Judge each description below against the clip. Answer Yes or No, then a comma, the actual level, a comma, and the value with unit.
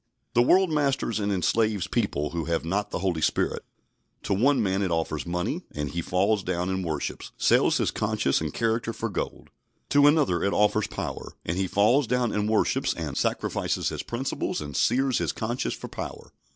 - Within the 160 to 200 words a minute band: Yes, average, 190 wpm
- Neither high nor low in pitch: No, low, 100 Hz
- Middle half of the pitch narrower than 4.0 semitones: No, average, 5.3 semitones